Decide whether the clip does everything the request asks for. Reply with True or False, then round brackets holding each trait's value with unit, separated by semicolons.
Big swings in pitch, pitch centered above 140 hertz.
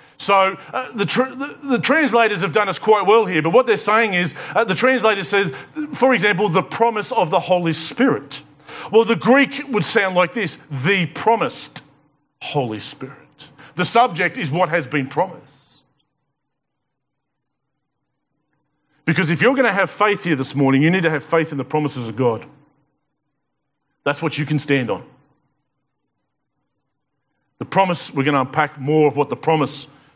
True (6.3 semitones; 155 Hz)